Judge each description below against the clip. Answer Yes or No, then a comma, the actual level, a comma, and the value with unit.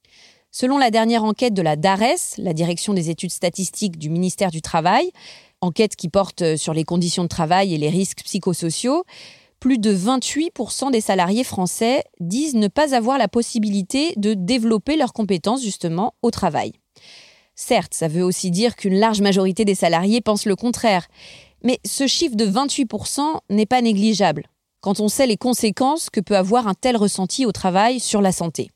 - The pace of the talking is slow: No, average, 175 wpm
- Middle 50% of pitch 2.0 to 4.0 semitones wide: No, average, 4.9 semitones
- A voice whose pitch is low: No, high, 210 Hz